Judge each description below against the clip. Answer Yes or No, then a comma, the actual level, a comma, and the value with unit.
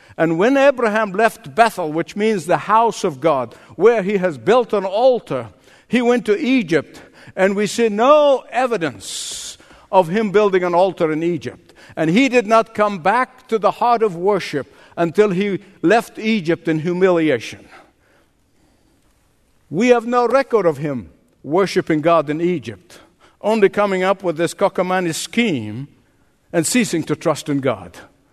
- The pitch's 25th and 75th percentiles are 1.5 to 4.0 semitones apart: No, wide, 5.4 semitones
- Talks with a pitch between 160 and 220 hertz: Yes, high, 190 Hz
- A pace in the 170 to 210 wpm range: No, average, 155 wpm